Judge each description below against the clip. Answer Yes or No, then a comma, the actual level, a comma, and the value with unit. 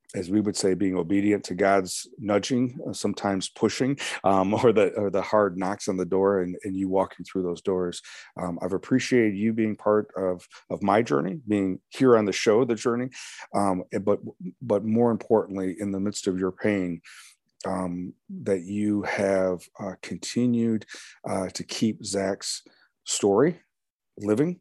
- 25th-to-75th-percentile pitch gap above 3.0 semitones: No, narrow, 2.4 semitones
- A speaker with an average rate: Yes, average, 165 wpm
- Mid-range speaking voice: No, low, 100 Hz